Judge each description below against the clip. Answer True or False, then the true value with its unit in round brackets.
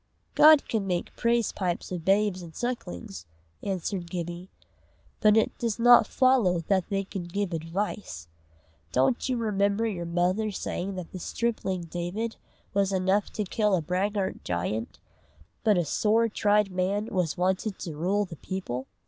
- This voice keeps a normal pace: True (155 wpm)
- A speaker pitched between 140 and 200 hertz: True (190 Hz)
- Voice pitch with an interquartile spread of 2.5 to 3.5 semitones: True (3.2 semitones)